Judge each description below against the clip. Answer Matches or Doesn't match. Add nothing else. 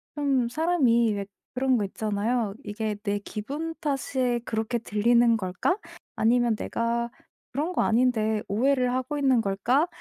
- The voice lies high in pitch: Matches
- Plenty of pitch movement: Doesn't match